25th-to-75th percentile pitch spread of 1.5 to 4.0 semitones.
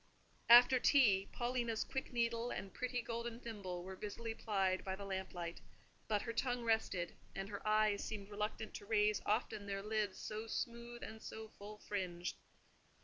Yes: average, 2.9 semitones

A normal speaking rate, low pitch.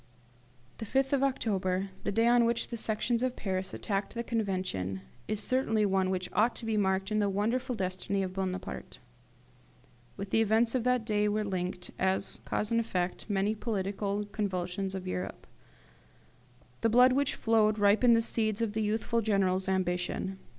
No: average, 170 wpm; high, 205 Hz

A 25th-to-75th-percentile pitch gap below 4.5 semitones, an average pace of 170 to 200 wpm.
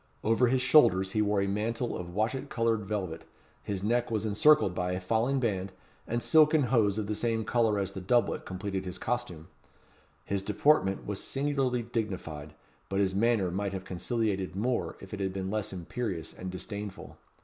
Yes: average, 3.7 semitones; average, 180 wpm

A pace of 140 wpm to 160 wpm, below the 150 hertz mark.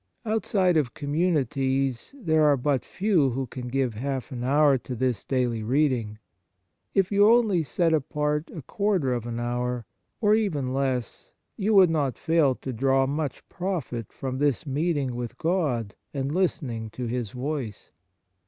Yes: average, 155 wpm; low, 135 Hz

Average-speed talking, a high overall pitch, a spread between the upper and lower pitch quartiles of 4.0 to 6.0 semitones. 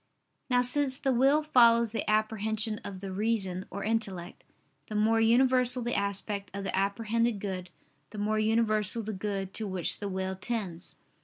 No: average, 165 wpm; high, 215 Hz; average, 2.8 semitones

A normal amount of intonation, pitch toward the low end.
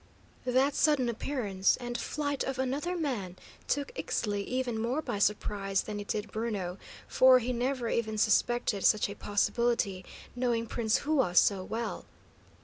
No: average, 3.9 semitones; high, 235 Hz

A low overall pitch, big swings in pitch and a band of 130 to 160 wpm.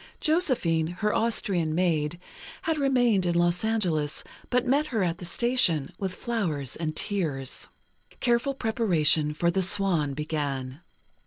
No: medium, 175 Hz; wide, 6.7 semitones; slow, 135 wpm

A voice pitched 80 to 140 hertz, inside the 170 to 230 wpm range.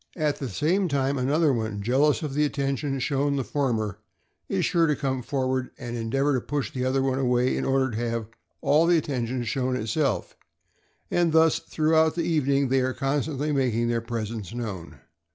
Yes: low, 135 Hz; average, 190 wpm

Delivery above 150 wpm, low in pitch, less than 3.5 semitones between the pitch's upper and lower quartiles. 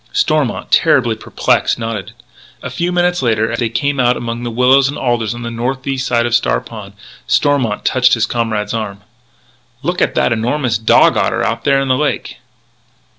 Yes: average, 180 wpm; low, 120 Hz; average, 2.9 semitones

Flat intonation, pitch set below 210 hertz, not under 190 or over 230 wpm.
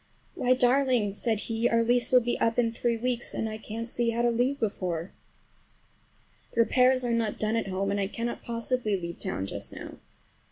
No: narrow, 2.3 semitones; high, 230 Hz; average, 200 wpm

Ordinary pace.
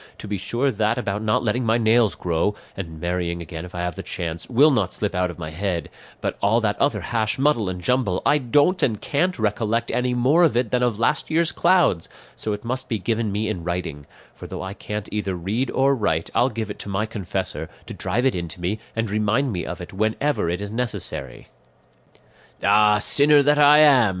No: fast, 220 wpm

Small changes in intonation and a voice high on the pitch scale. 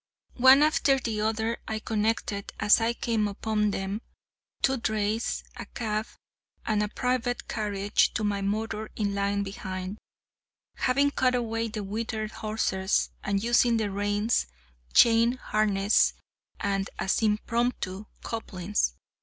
Yes: narrow, 2.3 semitones; high, 215 Hz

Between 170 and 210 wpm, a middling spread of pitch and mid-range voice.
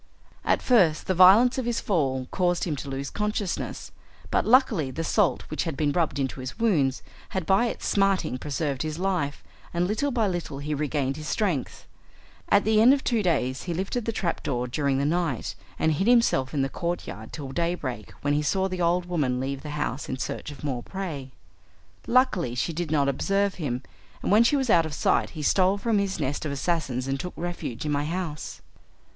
No: fast, 205 wpm; wide, 5.8 semitones; medium, 165 Hz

